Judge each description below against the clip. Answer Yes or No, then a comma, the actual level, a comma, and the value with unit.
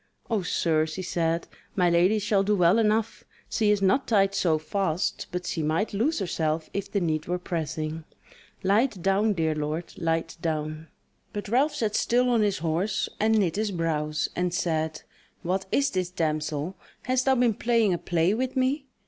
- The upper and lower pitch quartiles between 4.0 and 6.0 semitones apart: Yes, average, 4.7 semitones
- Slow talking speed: No, average, 180 wpm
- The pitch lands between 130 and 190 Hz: Yes, medium, 185 Hz